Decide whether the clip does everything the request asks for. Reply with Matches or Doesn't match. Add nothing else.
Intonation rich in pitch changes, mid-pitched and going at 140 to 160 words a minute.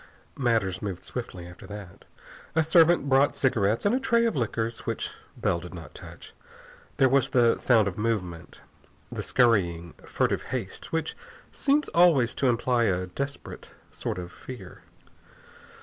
Doesn't match